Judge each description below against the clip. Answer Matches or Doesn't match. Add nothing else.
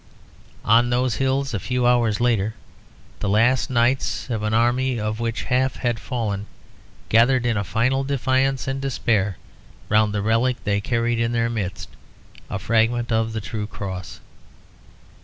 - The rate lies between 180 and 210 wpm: Doesn't match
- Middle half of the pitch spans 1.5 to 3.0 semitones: Matches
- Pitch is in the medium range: Doesn't match